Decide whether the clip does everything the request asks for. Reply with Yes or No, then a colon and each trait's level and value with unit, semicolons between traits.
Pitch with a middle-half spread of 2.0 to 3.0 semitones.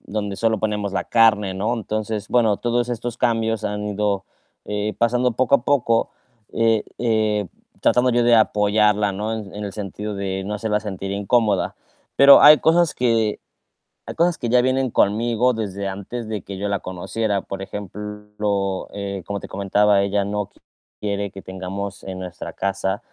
Yes: narrow, 2.4 semitones